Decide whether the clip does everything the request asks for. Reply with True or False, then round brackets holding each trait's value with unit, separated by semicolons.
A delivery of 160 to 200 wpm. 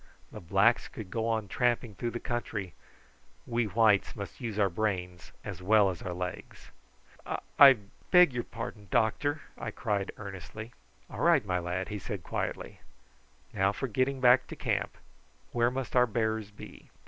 True (165 wpm)